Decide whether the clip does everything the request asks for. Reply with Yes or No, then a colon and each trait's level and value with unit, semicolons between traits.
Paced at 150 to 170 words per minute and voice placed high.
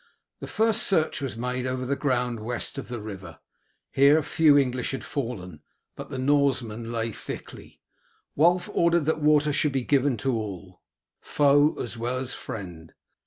No: average, 165 wpm; low, 130 Hz